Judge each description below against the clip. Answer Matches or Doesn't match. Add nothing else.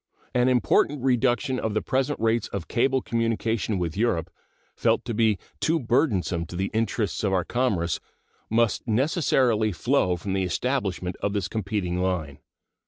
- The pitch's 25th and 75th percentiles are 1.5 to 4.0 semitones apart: Doesn't match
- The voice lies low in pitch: Matches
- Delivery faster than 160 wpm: Doesn't match